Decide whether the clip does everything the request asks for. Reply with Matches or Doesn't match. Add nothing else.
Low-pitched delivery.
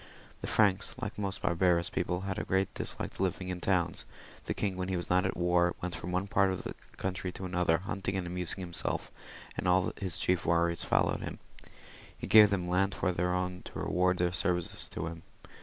Matches